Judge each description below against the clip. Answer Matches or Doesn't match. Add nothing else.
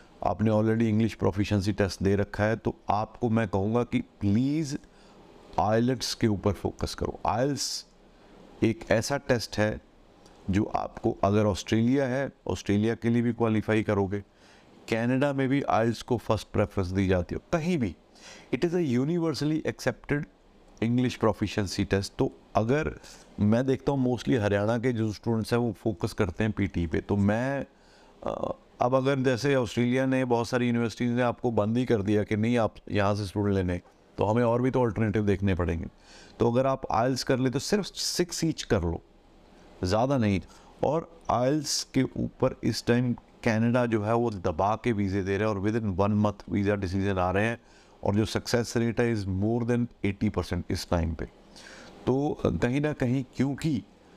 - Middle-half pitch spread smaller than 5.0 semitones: Matches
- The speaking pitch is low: Matches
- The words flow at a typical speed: Matches